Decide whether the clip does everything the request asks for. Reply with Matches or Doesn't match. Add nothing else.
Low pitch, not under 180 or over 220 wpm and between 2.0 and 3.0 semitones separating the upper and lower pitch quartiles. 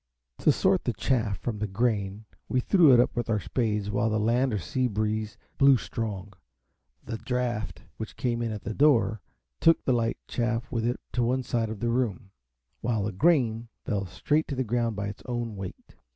Matches